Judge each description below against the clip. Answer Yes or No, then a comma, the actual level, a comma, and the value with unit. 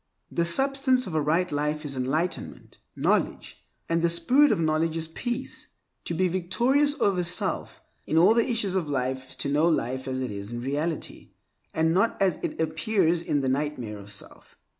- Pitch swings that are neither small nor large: Yes, average, 4.6 semitones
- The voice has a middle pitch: Yes, medium, 165 Hz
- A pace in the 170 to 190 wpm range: Yes, average, 185 wpm